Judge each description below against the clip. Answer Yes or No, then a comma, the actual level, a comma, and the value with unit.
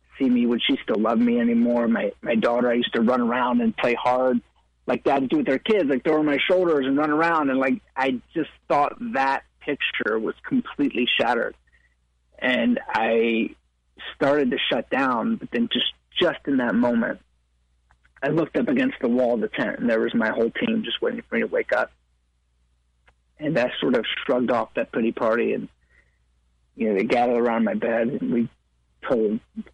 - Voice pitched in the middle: No, low, 120 Hz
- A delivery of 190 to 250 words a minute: Yes, average, 200 wpm